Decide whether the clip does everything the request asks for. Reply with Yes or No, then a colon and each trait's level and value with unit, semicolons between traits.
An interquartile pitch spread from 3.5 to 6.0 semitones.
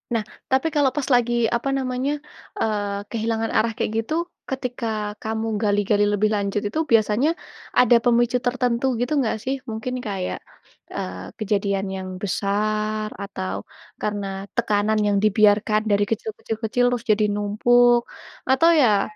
No: average, 2.9 semitones